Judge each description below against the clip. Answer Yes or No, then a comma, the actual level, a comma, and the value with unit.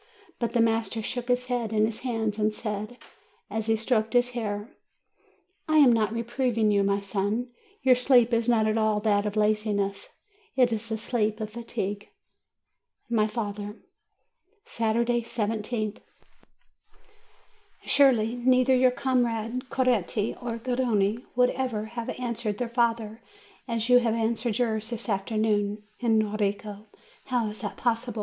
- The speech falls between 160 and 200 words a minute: No, average, 140 wpm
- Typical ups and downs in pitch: No, narrow, 2.3 semitones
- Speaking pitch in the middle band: No, high, 225 Hz